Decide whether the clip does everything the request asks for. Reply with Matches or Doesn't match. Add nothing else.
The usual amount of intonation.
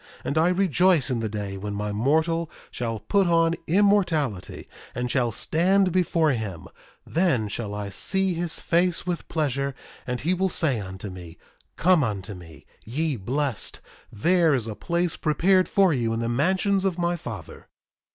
Doesn't match